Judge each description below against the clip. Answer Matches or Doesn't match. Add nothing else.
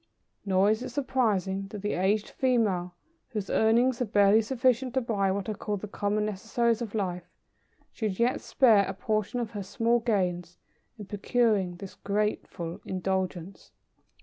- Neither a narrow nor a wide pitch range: Matches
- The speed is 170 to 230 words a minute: Doesn't match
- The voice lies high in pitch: Matches